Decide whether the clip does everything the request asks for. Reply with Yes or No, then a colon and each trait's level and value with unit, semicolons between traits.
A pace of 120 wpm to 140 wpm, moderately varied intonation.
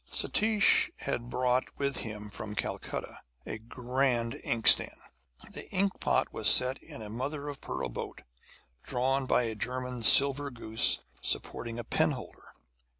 Yes: slow, 135 wpm; average, 3.1 semitones